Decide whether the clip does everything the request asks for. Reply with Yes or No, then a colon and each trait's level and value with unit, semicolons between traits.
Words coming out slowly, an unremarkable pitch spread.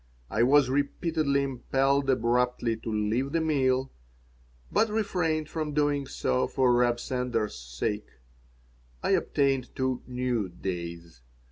Yes: slow, 120 wpm; average, 3.6 semitones